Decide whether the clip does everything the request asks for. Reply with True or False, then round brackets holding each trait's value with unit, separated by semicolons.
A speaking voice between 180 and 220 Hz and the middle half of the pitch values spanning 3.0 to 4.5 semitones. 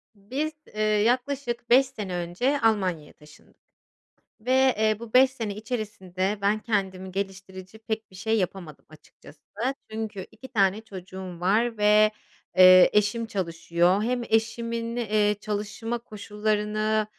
True (210 Hz; 3.3 semitones)